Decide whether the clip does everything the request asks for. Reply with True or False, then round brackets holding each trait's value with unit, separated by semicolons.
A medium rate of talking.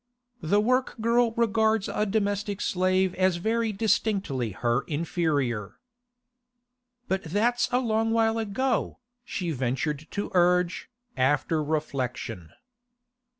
False (105 wpm)